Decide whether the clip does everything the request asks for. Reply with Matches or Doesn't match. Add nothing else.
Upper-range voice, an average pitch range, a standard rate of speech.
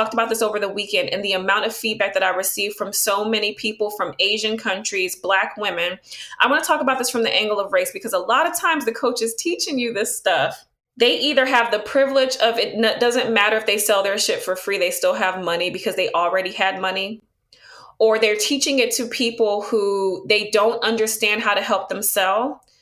Doesn't match